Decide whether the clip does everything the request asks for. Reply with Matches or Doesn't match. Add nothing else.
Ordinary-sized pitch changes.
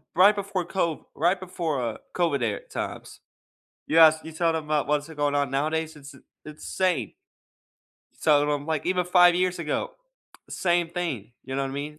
Matches